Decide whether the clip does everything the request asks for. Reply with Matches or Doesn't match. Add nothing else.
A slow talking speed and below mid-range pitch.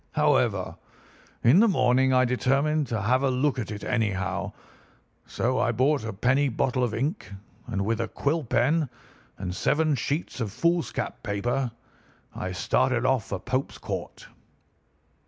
Doesn't match